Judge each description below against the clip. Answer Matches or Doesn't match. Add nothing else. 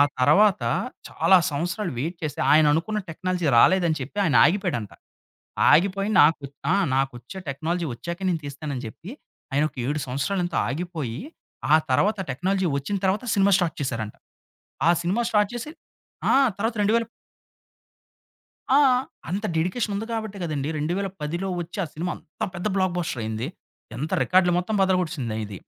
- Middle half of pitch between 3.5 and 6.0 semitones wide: Matches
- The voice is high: Doesn't match